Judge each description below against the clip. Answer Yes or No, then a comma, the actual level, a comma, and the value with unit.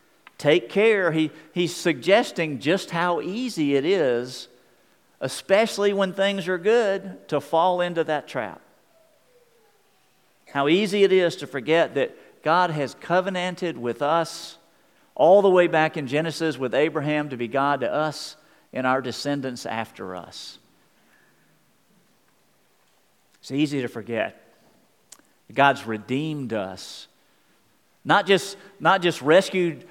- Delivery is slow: Yes, slow, 125 wpm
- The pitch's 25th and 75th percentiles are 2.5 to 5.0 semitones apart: No, wide, 5.5 semitones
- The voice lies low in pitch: No, medium, 165 Hz